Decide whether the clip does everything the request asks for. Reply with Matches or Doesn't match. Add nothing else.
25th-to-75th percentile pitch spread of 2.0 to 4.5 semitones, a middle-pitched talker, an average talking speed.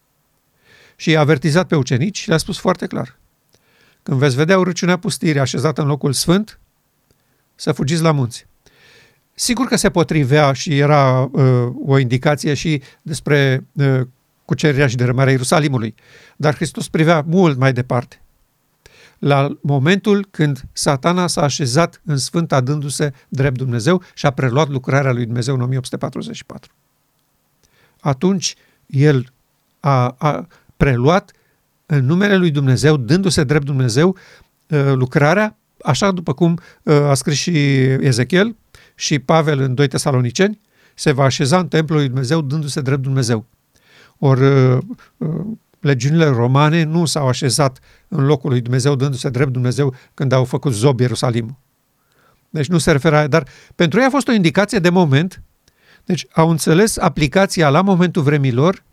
Matches